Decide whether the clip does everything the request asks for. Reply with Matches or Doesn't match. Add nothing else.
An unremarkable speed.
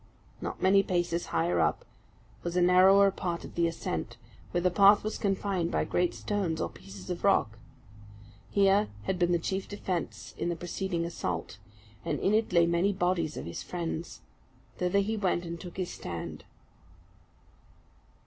Matches